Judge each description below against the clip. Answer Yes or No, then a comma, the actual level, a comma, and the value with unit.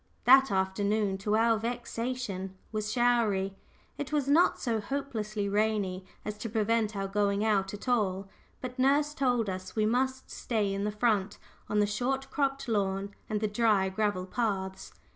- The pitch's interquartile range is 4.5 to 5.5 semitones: No, average, 3.5 semitones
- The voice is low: No, high, 215 Hz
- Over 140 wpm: Yes, average, 160 wpm